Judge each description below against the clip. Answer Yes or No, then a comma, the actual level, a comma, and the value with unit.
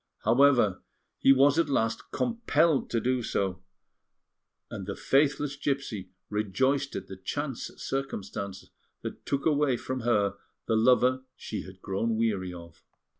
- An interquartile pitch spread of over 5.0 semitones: Yes, wide, 5.5 semitones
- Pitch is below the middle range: Yes, low, 120 Hz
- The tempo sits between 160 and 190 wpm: No, slow, 135 wpm